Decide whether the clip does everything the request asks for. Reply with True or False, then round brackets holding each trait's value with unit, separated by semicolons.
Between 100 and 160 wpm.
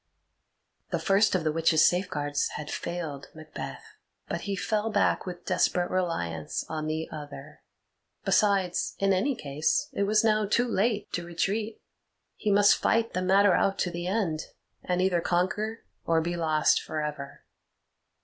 True (155 wpm)